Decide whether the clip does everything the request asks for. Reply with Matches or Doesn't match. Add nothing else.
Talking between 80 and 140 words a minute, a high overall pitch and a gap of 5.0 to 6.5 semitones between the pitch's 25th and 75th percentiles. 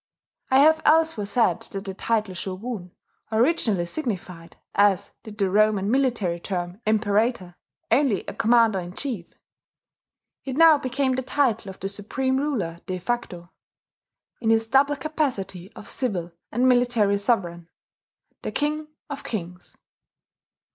Matches